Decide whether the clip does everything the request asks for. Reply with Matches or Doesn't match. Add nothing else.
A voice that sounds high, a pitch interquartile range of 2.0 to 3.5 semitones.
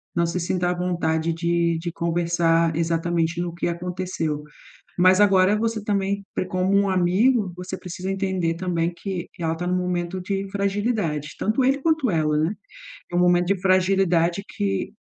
Doesn't match